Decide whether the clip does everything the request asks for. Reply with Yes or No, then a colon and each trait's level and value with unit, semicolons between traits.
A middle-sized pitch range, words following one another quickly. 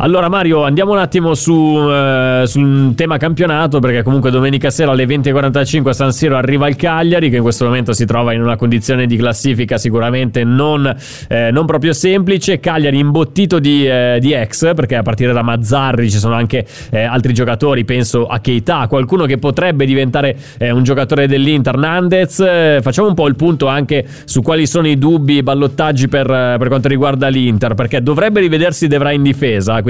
Yes: average, 3.8 semitones; fast, 190 wpm